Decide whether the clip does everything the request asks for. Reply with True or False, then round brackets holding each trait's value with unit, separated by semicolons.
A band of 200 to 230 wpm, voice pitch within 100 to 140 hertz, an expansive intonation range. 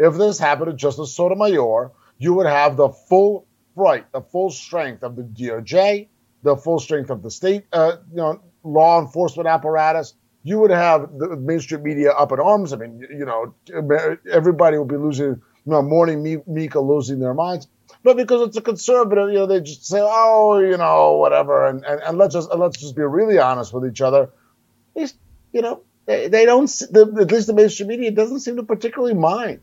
False (205 wpm; 165 Hz; 6.1 semitones)